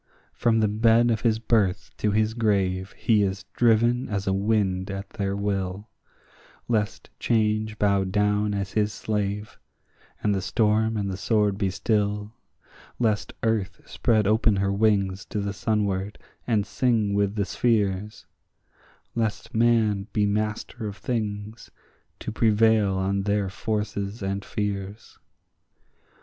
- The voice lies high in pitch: No, low, 105 Hz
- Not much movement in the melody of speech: Yes, narrow, 1.8 semitones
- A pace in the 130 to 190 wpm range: Yes, slow, 135 wpm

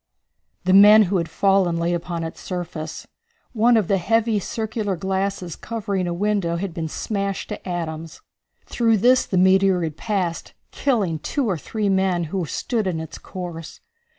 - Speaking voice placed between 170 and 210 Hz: Yes, high, 190 Hz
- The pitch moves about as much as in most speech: Yes, average, 3.4 semitones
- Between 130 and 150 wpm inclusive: No, average, 165 wpm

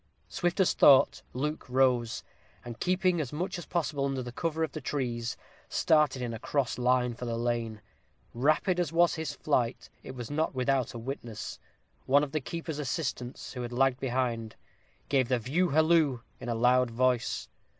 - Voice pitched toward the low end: Yes, low, 130 Hz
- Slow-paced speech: No, average, 175 wpm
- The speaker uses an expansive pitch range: No, average, 4.1 semitones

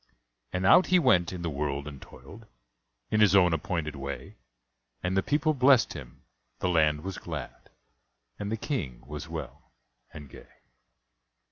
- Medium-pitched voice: No, very low, 90 Hz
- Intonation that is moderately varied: No, wide, 6.5 semitones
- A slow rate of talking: No, average, 155 wpm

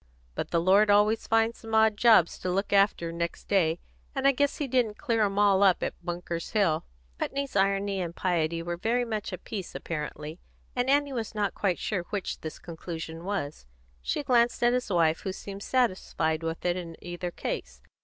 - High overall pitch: Yes, high, 195 Hz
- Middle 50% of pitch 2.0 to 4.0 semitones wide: No, average, 4.7 semitones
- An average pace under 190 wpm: No, average, 195 wpm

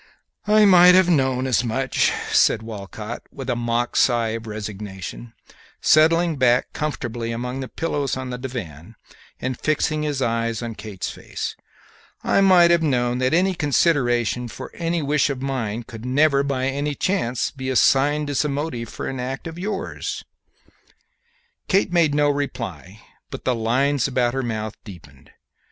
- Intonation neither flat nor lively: Yes, average, 4.2 semitones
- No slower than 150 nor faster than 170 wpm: Yes, average, 155 wpm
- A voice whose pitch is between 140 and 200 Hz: No, low, 130 Hz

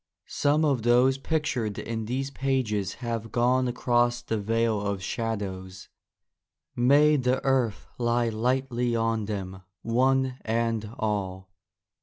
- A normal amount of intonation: Yes, average, 3.2 semitones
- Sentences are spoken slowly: Yes, slow, 120 wpm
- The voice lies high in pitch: No, low, 120 Hz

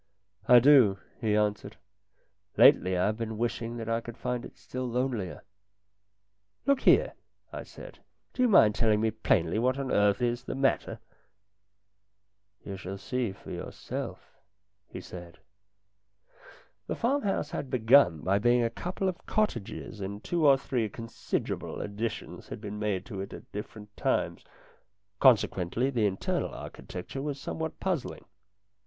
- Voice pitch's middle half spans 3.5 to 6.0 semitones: Yes, average, 4.2 semitones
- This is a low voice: Yes, low, 110 Hz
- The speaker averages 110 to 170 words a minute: Yes, average, 160 wpm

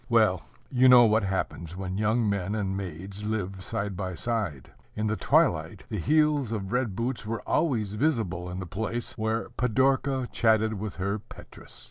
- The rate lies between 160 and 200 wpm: Yes, average, 170 wpm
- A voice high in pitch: No, low, 110 Hz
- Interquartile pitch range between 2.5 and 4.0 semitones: Yes, average, 3.7 semitones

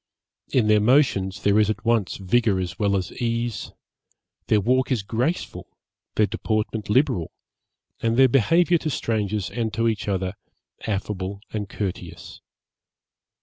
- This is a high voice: No, low, 110 Hz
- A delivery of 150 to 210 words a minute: No, average, 140 wpm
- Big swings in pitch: No, average, 3.1 semitones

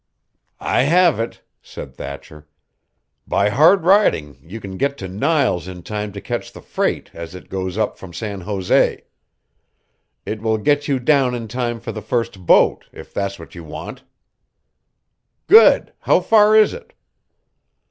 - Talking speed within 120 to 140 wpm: No, average, 160 wpm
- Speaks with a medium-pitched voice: No, low, 110 Hz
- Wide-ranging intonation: Yes, wide, 7.3 semitones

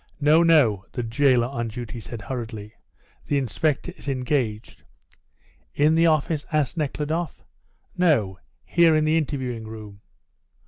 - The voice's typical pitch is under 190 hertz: Yes, low, 135 Hz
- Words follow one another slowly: Yes, slow, 130 wpm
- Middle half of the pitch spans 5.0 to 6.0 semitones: Yes, average, 5.3 semitones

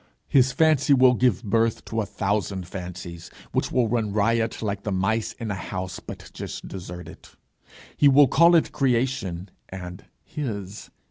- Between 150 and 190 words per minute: Yes, average, 155 wpm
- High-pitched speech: No, low, 110 Hz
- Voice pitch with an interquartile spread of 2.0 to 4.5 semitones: No, average, 5.0 semitones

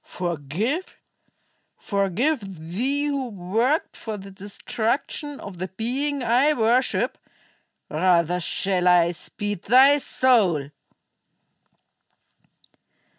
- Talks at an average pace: No, slow, 85 wpm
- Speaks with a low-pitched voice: No, high, 205 Hz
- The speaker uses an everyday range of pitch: No, wide, 6.4 semitones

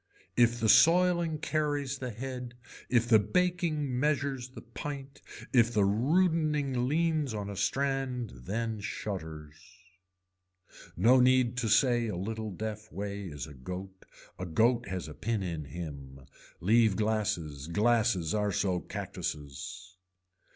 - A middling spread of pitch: No, wide, 5.9 semitones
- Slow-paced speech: Yes, slow, 130 wpm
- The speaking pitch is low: Yes, low, 110 Hz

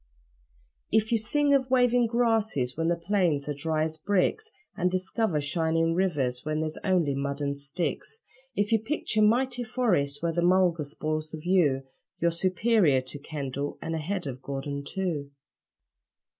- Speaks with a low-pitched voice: No, medium, 170 Hz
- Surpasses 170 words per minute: No, average, 155 wpm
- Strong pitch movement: Yes, wide, 6.5 semitones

